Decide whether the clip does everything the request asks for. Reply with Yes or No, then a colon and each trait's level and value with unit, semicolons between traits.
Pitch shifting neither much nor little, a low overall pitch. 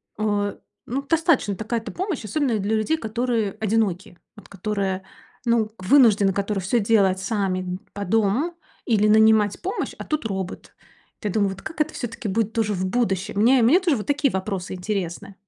No: average, 3.4 semitones; high, 215 Hz